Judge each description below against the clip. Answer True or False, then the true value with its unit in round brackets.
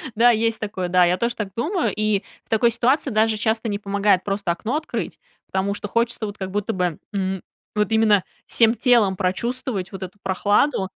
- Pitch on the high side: True (210 Hz)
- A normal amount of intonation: True (3.2 semitones)